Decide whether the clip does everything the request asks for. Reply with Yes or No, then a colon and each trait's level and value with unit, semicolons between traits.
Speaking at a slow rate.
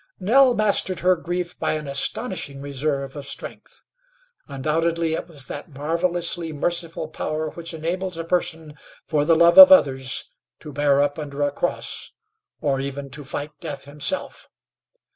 No: average, 150 wpm